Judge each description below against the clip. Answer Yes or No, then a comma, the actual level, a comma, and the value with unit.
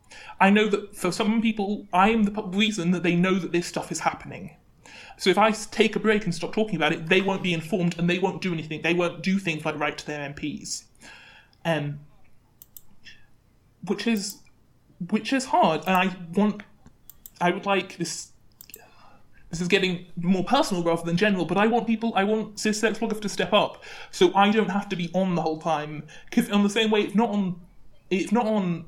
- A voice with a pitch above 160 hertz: Yes, medium, 185 Hz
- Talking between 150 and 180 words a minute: No, average, 200 wpm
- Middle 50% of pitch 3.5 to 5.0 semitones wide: Yes, average, 4.2 semitones